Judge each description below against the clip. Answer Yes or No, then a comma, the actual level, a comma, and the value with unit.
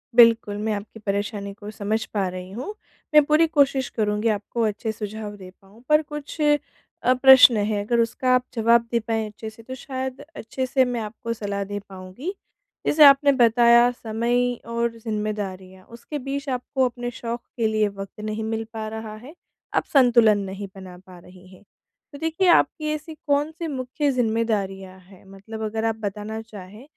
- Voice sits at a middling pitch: No, high, 225 Hz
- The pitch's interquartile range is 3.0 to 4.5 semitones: Yes, average, 3.7 semitones